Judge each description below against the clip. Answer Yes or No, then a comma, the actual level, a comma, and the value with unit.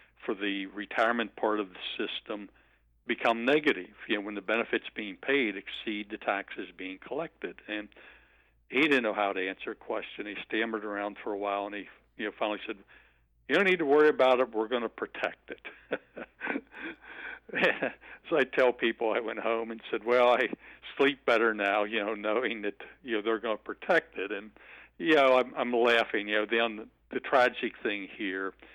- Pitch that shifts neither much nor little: No, narrow, 2.3 semitones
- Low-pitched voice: Yes, low, 110 Hz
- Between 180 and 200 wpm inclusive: Yes, average, 190 wpm